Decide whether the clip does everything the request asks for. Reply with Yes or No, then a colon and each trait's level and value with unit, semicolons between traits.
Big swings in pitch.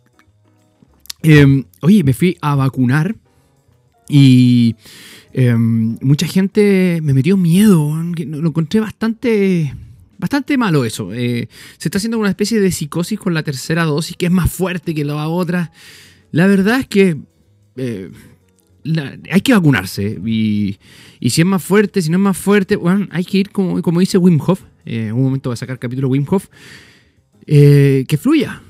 Yes: wide, 7.3 semitones